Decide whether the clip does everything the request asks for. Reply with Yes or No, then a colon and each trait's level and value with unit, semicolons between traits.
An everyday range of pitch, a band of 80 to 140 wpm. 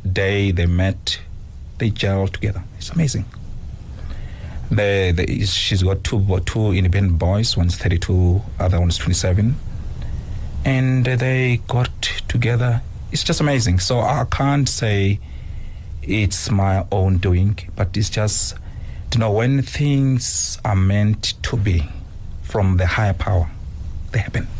Yes: average, 3.8 semitones; slow, 135 wpm